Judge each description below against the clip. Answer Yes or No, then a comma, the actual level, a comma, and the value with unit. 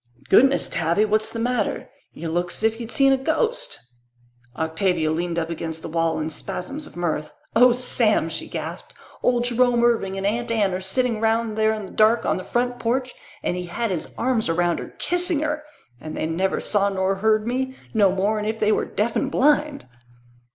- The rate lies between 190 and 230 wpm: Yes, average, 195 wpm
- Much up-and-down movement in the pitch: Yes, wide, 5.7 semitones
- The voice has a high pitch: Yes, high, 215 Hz